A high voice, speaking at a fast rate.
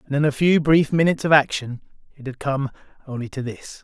No: medium, 140 Hz; fast, 220 wpm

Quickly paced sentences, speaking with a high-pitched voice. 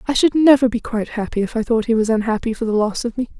Yes: fast, 300 wpm; high, 230 Hz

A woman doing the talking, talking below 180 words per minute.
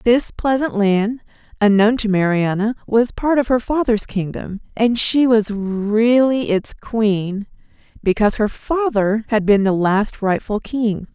Yes: female; average, 145 wpm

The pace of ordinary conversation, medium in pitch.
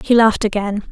No: average, 195 wpm; high, 215 Hz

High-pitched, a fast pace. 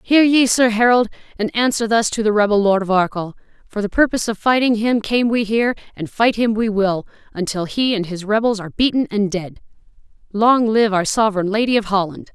Yes: high, 215 Hz; fast, 210 wpm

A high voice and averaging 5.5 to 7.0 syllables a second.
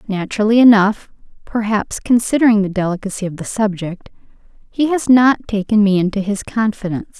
Yes: high, 210 Hz; 5.7 syllables/s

